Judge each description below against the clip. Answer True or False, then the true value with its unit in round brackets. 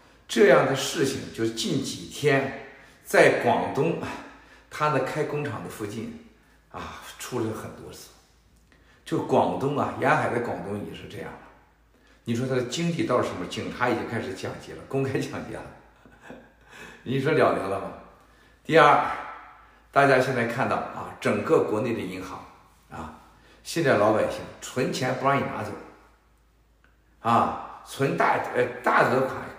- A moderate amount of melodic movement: True (4.3 semitones)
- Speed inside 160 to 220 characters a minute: True (205 characters per minute)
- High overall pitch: False (130 Hz)